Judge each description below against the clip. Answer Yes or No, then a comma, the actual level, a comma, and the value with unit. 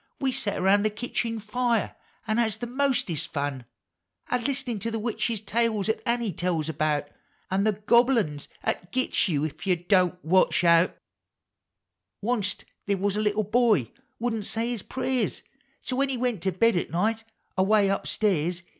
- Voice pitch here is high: Yes, high, 210 Hz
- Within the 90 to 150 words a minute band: No, average, 175 wpm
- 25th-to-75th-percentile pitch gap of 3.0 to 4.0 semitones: No, average, 4.6 semitones